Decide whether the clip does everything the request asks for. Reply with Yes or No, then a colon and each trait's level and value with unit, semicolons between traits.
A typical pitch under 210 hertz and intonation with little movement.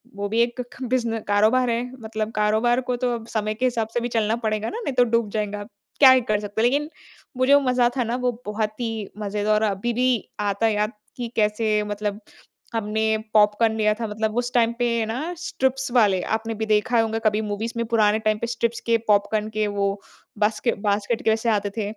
No: high, 220 Hz; narrow, 2.0 semitones